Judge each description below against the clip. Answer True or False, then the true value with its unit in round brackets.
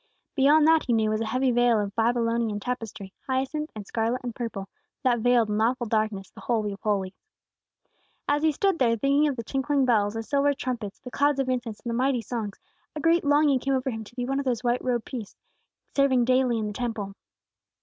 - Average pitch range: True (3.5 semitones)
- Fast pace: True (215 wpm)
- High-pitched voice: True (245 Hz)